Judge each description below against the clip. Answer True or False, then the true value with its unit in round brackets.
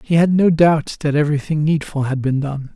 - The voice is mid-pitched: True (150 Hz)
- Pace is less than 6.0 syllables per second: True (5.5 syllables/s)